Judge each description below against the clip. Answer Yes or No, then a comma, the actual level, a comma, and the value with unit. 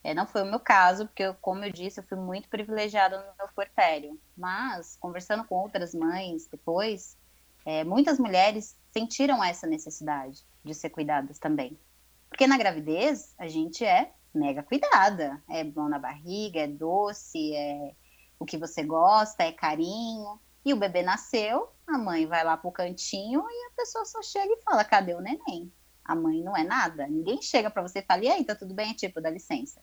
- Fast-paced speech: Yes, fast, 190 wpm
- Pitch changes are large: Yes, wide, 6.0 semitones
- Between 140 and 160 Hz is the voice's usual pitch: No, high, 190 Hz